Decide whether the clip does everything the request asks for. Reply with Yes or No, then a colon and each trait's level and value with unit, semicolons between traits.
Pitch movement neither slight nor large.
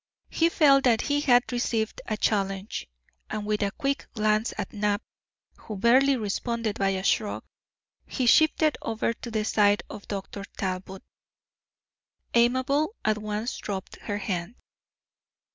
Yes: average, 3.3 semitones